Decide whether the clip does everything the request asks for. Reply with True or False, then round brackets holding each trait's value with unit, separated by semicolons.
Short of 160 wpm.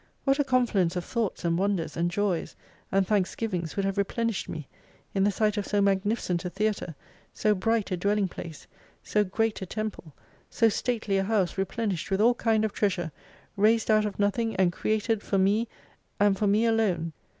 False (190 wpm)